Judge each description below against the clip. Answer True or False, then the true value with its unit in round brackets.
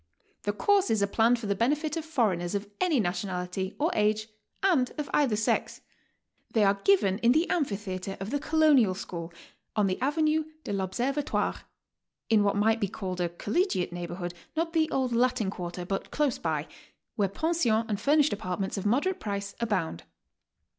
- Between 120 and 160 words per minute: False (175 wpm)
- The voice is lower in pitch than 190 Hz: False (215 Hz)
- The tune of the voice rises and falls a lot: True (7.0 semitones)